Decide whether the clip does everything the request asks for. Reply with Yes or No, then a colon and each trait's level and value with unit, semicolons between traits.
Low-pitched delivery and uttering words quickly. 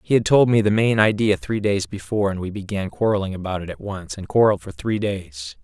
Yes: low, 100 Hz; fast, 245 wpm